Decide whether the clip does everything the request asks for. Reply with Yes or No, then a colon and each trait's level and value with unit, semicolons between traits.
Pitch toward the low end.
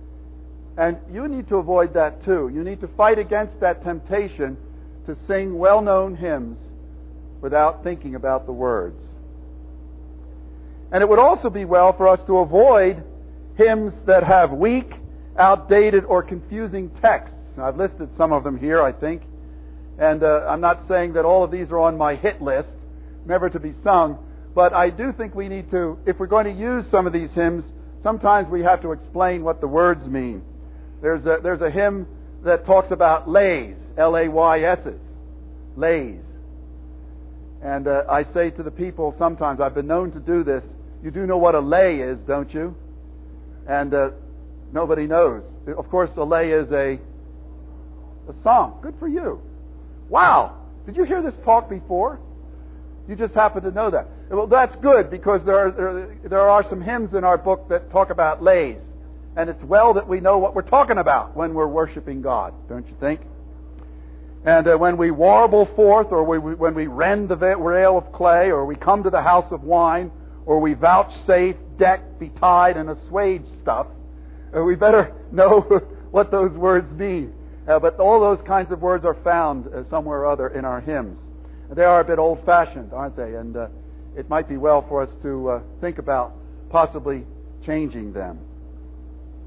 No: medium, 165 Hz